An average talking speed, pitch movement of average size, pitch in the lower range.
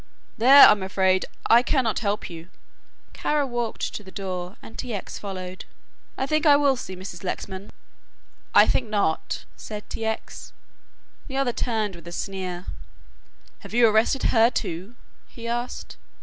No: average, 155 wpm; average, 4.3 semitones; high, 215 Hz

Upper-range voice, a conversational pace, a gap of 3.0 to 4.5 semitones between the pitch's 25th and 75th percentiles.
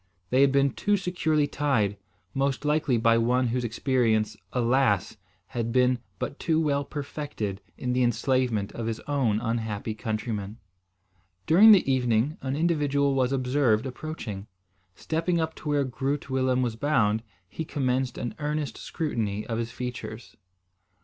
No: low, 130 Hz; average, 145 wpm; average, 4.1 semitones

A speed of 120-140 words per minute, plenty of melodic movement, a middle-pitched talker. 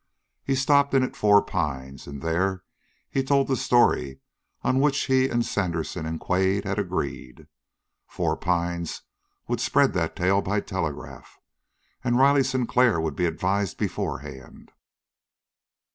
No: slow, 135 wpm; wide, 7.6 semitones; very low, 95 Hz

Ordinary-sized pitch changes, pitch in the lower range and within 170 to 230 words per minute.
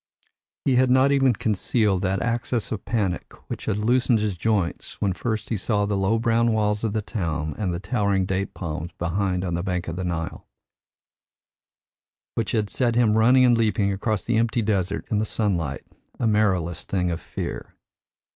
Yes: average, 3.8 semitones; low, 105 Hz; average, 185 wpm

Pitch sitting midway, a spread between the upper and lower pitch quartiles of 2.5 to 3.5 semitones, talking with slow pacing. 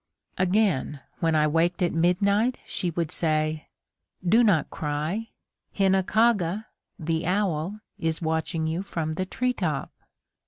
No: medium, 175 Hz; average, 4.0 semitones; slow, 125 wpm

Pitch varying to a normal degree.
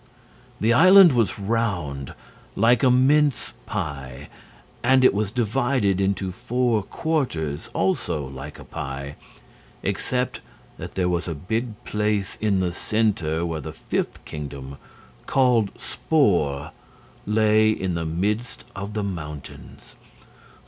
No: wide, 6.4 semitones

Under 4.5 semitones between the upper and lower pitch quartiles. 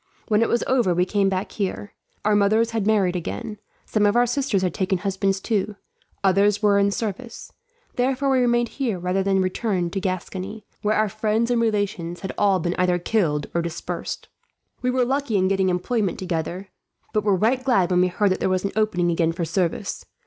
Yes: average, 3.1 semitones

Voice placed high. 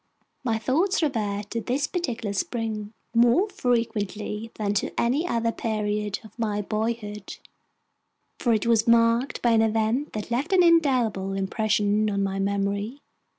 Yes: high, 225 Hz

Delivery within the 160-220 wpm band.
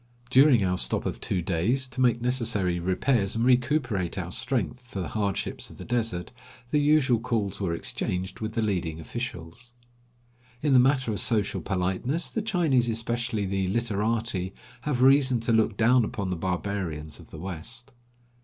Yes: average, 165 wpm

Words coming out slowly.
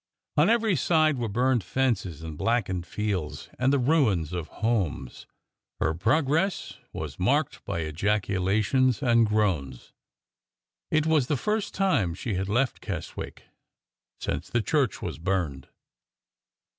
Yes: slow, 130 wpm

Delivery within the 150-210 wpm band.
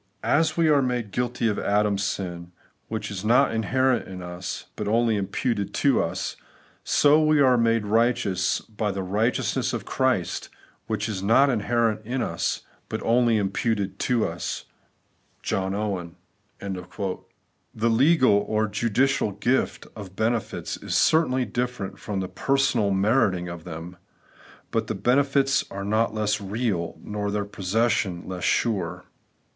No: average, 140 wpm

